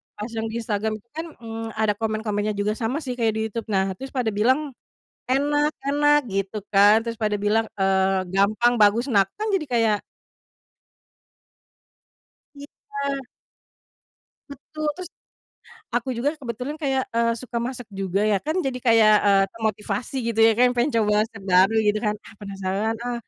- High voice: Yes, high, 225 Hz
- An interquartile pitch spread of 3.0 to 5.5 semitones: Yes, average, 3.7 semitones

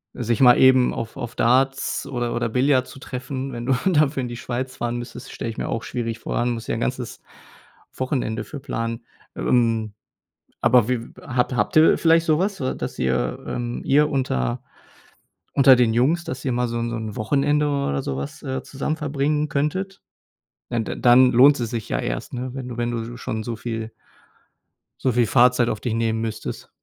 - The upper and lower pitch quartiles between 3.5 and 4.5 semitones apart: No, average, 2.7 semitones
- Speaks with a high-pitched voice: No, low, 125 Hz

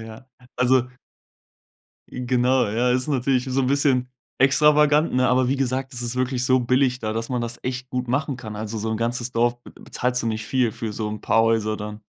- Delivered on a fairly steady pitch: Yes, narrow, 2.3 semitones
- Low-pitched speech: Yes, low, 125 Hz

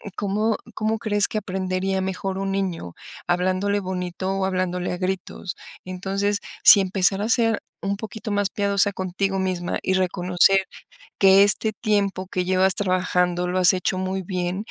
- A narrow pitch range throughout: Yes, narrow, 1.6 semitones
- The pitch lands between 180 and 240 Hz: Yes, high, 190 Hz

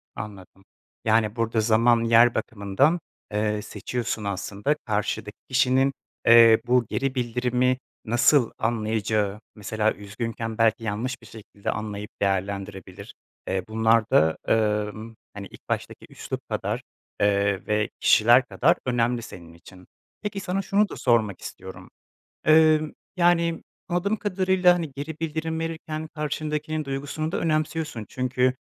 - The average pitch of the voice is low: Yes, low, 115 Hz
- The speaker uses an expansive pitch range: Yes, wide, 6.3 semitones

